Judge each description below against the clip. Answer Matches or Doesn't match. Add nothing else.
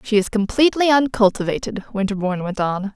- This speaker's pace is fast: Doesn't match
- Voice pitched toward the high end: Matches